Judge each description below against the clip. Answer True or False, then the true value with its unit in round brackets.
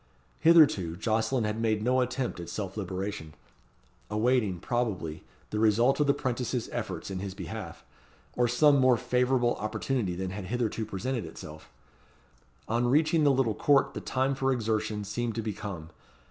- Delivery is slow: False (160 wpm)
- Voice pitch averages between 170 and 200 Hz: False (115 Hz)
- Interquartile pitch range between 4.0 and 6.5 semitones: True (4.3 semitones)